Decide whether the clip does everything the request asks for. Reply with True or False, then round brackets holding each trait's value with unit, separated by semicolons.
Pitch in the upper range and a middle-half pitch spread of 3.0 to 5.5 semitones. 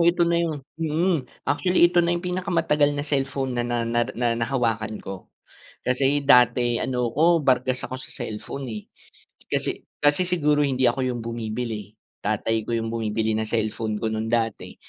False (125 Hz; 4.5 semitones)